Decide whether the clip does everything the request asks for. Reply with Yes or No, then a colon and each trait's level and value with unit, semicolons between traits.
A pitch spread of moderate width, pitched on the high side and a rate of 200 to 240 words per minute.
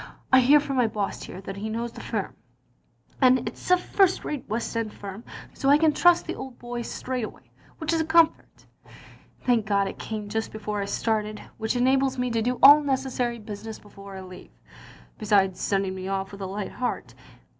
Yes: average, 4.4 semitones; high, 230 Hz; fast, 205 wpm